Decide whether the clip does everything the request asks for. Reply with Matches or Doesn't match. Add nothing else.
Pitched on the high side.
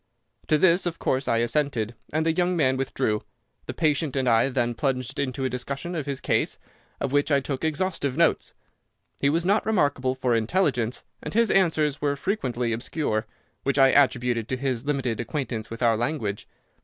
Doesn't match